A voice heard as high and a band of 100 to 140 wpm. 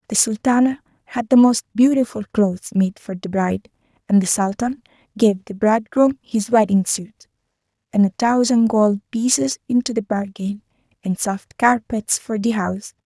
No: high, 220 Hz; average, 155 wpm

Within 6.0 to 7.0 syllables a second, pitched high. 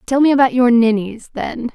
No: 5.2 syllables/s; high, 240 Hz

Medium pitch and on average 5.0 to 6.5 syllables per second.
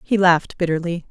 Yes: medium, 175 Hz; 5.9 syllables/s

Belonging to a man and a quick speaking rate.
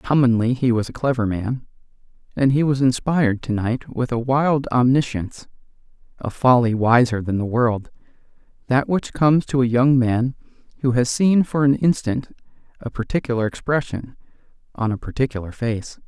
No: male; average, 155 wpm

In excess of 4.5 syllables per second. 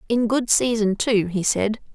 No: 4.2 syllables/s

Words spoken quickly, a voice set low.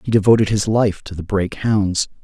Yes: fast, 215 wpm; low, 105 Hz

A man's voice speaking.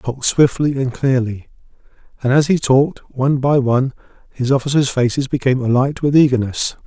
Yes: male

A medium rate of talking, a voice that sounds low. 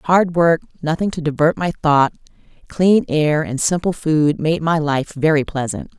No: average, 170 wpm; medium, 160 Hz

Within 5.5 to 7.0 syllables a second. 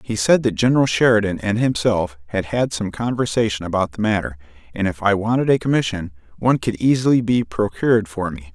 Yes: 5.8 syllables/s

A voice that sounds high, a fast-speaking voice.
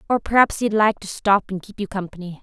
Yes: high, 200 Hz; fast, 250 wpm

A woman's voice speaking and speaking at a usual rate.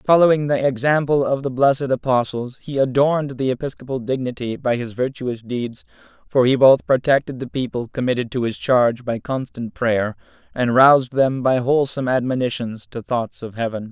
No: male; average, 170 wpm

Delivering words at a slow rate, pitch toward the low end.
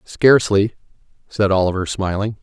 Yes: slow, 100 wpm; low, 100 Hz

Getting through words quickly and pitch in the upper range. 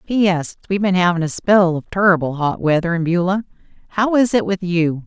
No: fast, 215 wpm; medium, 180 Hz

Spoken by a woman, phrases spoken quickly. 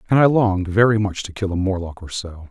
No: male; fast, 265 wpm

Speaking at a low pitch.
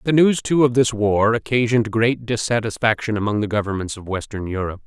Yes: low, 110 Hz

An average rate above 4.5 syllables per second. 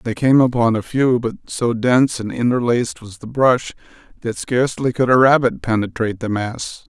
Yes: 5.2 syllables/s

